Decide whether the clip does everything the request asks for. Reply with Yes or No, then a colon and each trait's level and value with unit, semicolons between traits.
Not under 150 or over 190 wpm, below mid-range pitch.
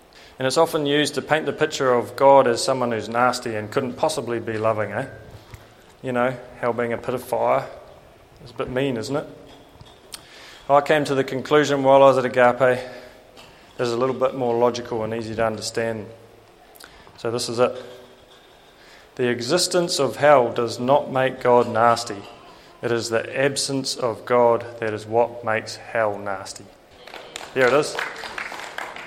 Yes: average, 170 wpm; low, 125 Hz